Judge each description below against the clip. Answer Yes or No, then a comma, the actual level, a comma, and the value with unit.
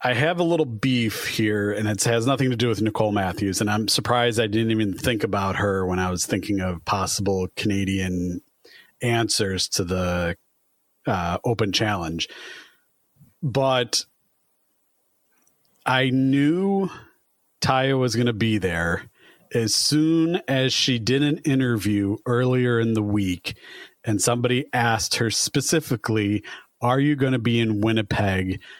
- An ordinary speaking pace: Yes, average, 145 wpm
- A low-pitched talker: Yes, low, 115 Hz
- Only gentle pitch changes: No, average, 4.4 semitones